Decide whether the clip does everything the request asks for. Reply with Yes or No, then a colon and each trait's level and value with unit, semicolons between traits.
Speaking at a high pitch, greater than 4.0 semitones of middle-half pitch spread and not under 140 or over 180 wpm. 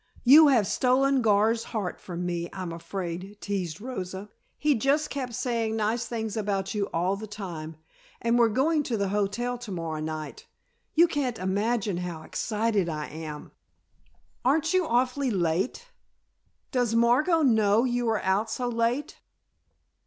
Yes: high, 220 Hz; average, 4.7 semitones; average, 150 wpm